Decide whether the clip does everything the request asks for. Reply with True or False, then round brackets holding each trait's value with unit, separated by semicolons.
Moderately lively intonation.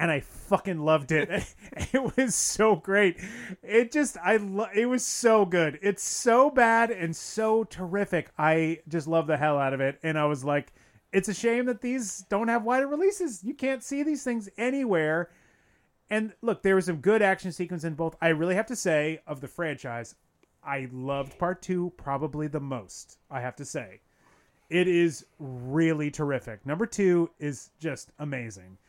False (6.5 semitones)